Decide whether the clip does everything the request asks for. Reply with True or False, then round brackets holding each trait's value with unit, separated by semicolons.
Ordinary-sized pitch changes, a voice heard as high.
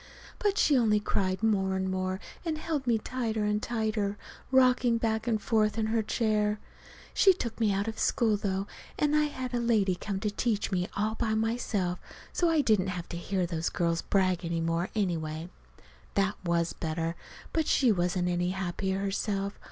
True (3.6 semitones; 210 Hz)